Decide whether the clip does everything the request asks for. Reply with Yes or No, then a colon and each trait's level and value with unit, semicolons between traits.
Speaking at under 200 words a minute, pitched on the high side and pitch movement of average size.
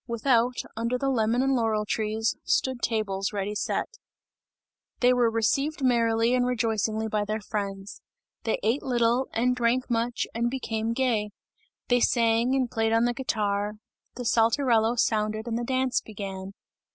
No: average, 150 wpm; high, 230 Hz; narrow, 2.3 semitones